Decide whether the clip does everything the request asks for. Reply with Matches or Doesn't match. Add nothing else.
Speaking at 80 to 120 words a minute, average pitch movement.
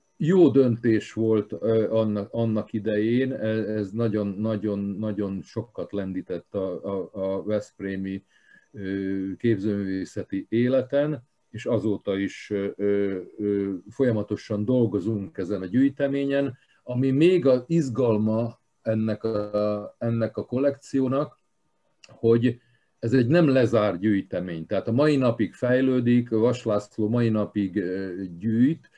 Matches